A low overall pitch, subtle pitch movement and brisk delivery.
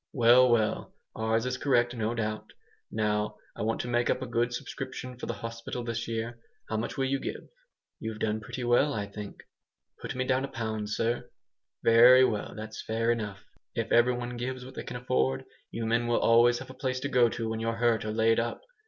Yes: low, 115 Hz; narrow, 1.8 semitones; fast, 215 wpm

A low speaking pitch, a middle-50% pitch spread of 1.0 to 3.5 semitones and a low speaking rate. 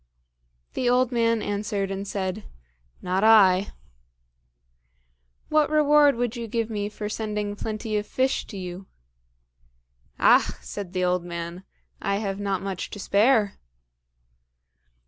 No: high, 205 Hz; average, 3.0 semitones; slow, 125 wpm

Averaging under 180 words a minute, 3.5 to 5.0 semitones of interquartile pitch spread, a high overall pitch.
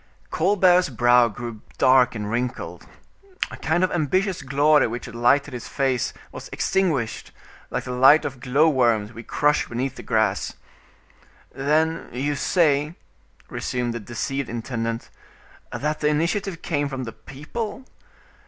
No: average, 140 wpm; average, 4.4 semitones; low, 135 Hz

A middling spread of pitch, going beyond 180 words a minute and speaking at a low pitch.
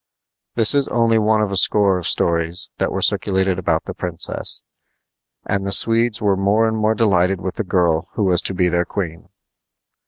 Yes: average, 3.4 semitones; average, 190 wpm; very low, 95 Hz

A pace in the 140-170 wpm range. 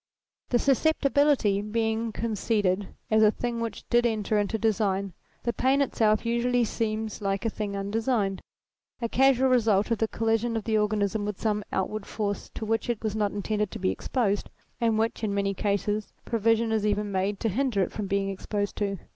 No: average, 185 wpm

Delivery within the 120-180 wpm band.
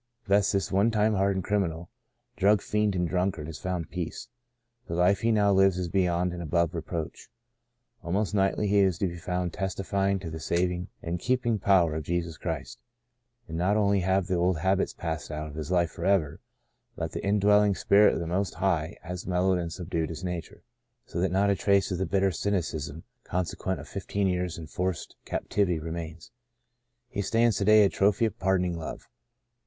No: average, 190 wpm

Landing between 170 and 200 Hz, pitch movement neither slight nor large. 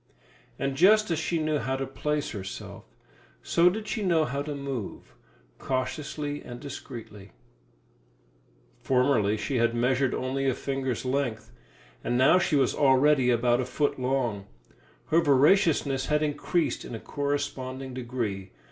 No: low, 135 Hz; average, 3.1 semitones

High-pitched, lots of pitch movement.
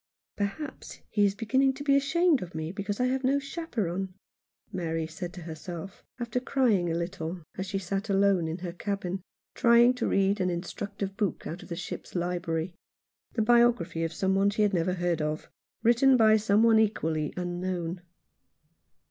No: high, 195 Hz; average, 4.7 semitones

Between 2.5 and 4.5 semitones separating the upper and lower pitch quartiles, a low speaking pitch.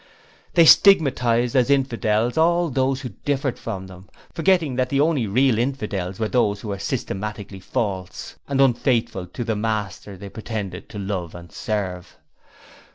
No: average, 5.1 semitones; low, 115 Hz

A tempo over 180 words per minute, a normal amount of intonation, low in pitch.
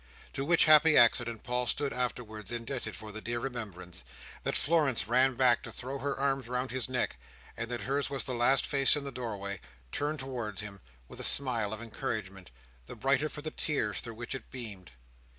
Yes: average, 195 wpm; average, 3.7 semitones; low, 125 Hz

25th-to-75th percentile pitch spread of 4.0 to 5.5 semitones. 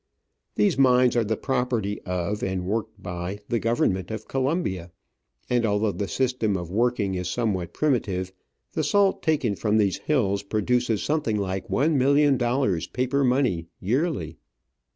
Yes: average, 4.9 semitones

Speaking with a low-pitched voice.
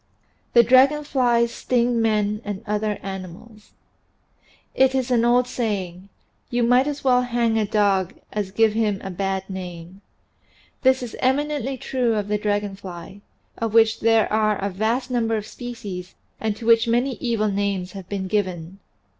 No: high, 220 Hz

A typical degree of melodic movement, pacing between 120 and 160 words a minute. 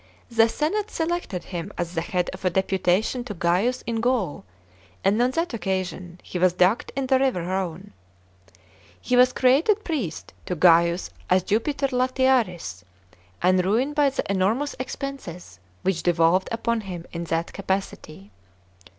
No: wide, 6.2 semitones; average, 150 wpm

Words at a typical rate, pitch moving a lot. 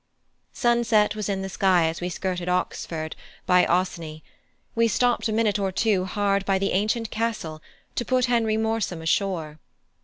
No: average, 160 wpm; average, 3.8 semitones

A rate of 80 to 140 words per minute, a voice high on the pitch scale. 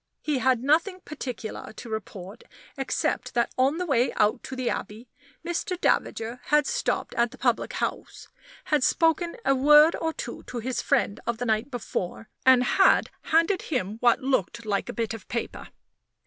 No: average, 175 wpm; very high, 255 Hz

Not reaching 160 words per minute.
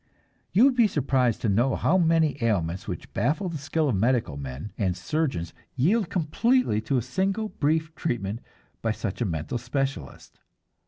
No: average, 165 wpm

